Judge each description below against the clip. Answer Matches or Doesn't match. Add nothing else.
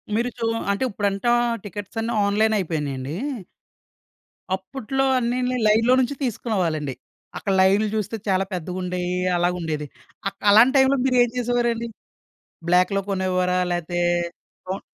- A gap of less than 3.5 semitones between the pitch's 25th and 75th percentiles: Doesn't match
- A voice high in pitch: Matches